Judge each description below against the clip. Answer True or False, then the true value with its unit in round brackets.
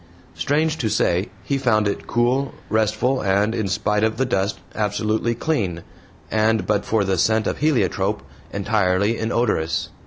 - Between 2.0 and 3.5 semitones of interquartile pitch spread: True (3.0 semitones)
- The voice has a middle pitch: False (110 Hz)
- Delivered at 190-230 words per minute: False (150 wpm)